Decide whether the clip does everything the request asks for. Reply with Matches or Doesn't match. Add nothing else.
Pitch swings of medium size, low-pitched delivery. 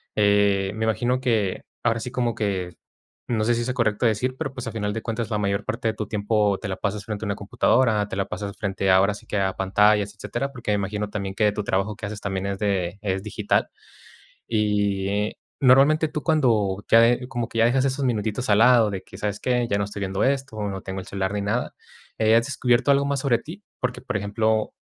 Matches